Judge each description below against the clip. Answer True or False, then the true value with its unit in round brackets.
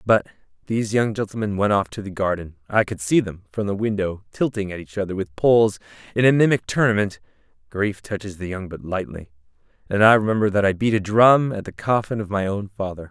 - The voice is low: True (100 Hz)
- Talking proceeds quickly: True (215 wpm)